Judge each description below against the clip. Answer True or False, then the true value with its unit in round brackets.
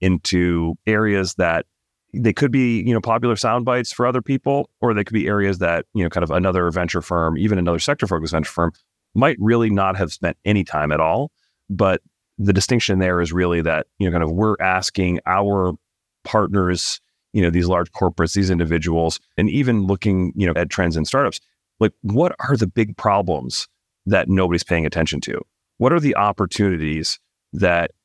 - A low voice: True (95 Hz)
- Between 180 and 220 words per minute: True (190 wpm)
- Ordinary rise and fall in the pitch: True (4.0 semitones)